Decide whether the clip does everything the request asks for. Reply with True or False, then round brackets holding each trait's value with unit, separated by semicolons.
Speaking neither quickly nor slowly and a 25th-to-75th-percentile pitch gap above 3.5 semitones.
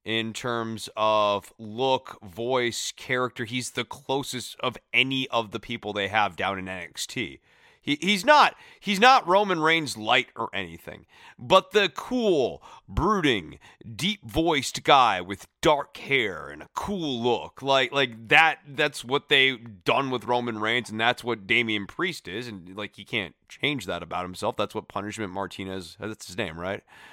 True (165 wpm; 4.5 semitones)